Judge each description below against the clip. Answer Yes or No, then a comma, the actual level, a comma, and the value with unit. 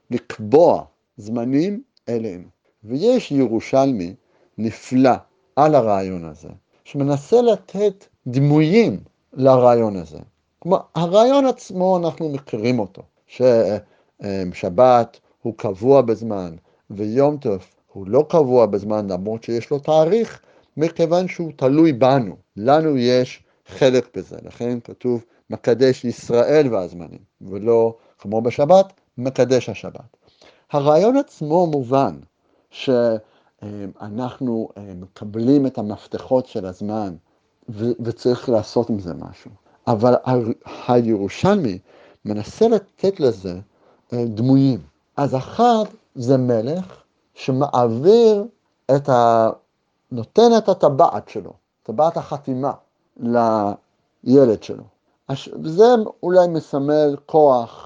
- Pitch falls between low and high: No, low, 125 Hz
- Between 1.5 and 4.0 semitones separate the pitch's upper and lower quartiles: No, average, 5.3 semitones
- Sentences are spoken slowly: Yes, slow, 95 wpm